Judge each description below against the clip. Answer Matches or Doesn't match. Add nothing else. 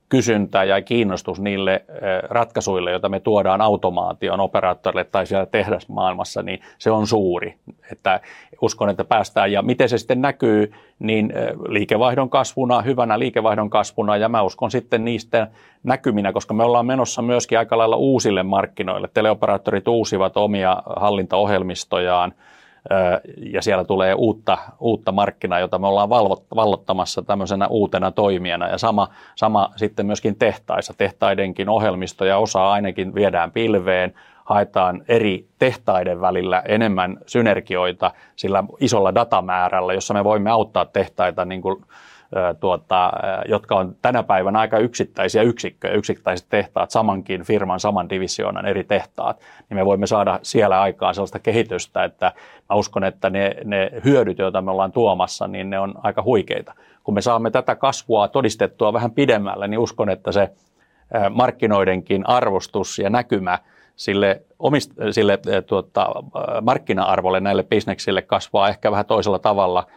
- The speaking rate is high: Doesn't match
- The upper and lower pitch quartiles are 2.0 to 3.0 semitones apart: Matches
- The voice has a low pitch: Matches